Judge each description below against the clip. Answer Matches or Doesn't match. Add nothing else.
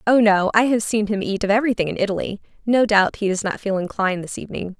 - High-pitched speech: Matches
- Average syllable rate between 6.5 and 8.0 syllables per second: Matches